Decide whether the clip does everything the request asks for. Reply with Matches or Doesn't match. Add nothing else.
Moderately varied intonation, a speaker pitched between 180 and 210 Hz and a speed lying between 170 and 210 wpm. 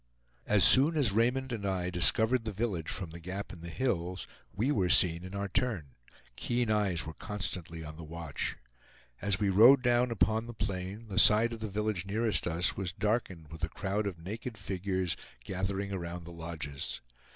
Doesn't match